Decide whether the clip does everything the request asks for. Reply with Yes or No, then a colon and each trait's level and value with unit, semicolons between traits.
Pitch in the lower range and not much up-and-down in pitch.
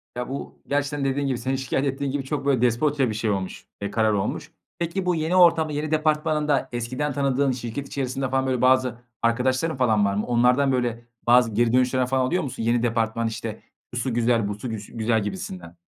No: low, 125 Hz; average, 3.3 semitones